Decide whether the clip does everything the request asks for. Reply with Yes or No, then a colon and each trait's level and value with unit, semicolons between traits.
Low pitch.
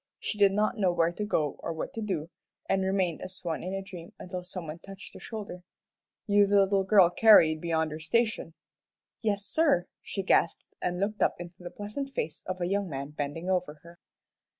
No: medium, 185 Hz